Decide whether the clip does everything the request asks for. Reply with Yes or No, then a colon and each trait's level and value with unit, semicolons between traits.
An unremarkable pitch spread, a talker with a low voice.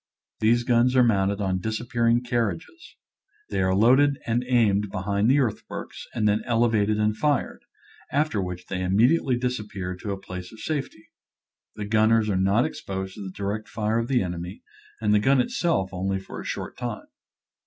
Yes: average, 3.7 semitones; low, 110 Hz